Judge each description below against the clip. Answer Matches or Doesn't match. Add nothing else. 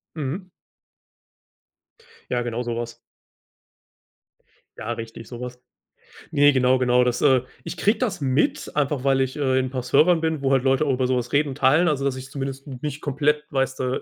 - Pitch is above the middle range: Doesn't match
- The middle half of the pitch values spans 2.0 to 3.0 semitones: Matches